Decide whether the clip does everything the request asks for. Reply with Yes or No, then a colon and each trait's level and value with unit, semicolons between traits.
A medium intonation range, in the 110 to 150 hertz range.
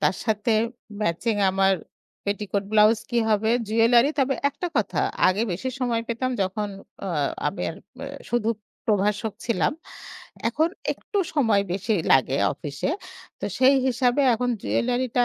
No: average, 3.5 semitones; high, 225 Hz